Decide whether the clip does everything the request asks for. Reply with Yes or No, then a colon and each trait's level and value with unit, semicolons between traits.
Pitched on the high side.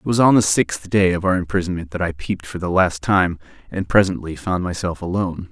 No: very low, 90 Hz